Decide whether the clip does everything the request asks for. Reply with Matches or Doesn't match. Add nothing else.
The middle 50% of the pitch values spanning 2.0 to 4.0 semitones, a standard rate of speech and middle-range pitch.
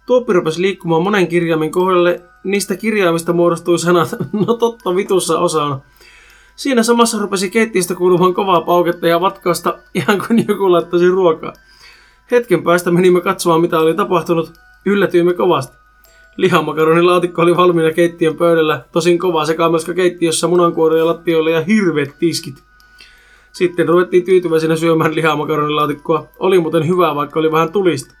Matches